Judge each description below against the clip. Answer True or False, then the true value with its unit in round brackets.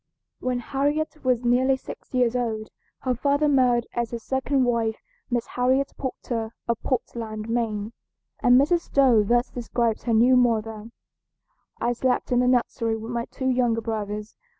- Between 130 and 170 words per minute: True (155 wpm)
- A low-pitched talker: False (240 Hz)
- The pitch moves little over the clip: True (2.2 semitones)